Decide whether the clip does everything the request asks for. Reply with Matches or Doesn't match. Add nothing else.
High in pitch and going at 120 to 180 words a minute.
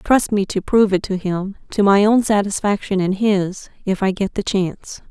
Doesn't match